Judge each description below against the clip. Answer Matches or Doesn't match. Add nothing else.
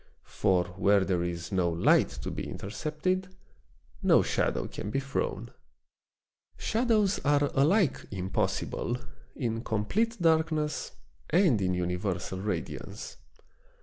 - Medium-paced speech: Doesn't match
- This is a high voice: Doesn't match